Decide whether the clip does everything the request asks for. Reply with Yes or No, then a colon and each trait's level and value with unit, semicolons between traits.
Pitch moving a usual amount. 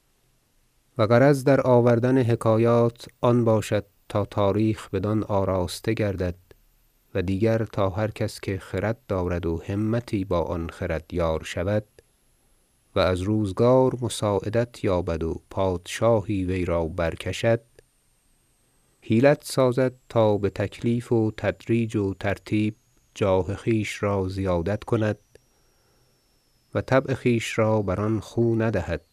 Yes: average, 3.5 semitones